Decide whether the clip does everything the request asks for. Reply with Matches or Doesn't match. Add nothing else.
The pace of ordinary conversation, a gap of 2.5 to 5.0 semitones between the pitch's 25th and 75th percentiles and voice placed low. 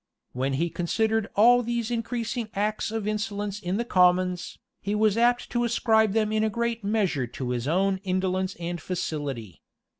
Doesn't match